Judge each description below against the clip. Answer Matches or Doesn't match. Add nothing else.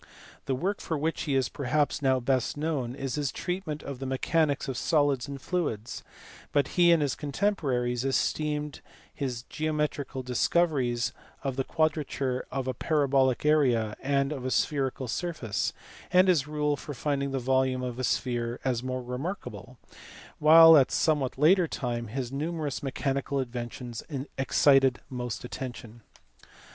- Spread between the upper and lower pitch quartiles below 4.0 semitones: Matches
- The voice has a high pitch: Doesn't match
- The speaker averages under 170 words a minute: Matches